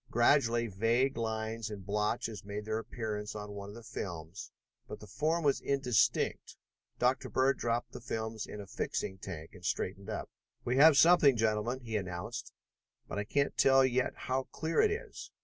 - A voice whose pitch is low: Yes, low, 115 Hz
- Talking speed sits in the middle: Yes, average, 175 wpm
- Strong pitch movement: No, average, 3.9 semitones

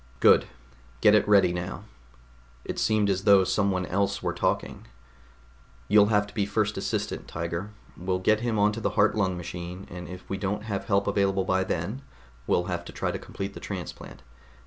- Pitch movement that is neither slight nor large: No, narrow, 2.2 semitones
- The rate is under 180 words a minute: No, average, 185 wpm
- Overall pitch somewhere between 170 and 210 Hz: No, low, 100 Hz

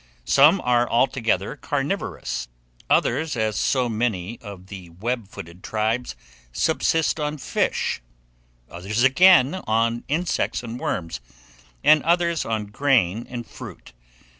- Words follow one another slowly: Yes, slow, 115 wpm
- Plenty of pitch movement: Yes, wide, 5.7 semitones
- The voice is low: Yes, low, 120 Hz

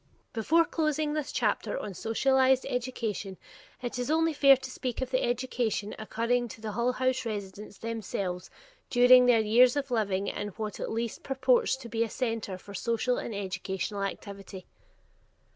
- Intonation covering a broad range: No, average, 3.8 semitones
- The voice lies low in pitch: No, high, 235 Hz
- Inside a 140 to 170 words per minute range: Yes, average, 160 wpm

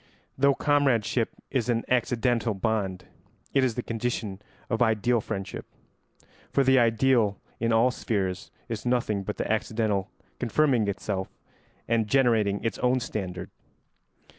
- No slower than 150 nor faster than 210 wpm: No, slow, 135 wpm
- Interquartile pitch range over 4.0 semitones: No, average, 3.1 semitones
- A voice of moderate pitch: No, low, 115 Hz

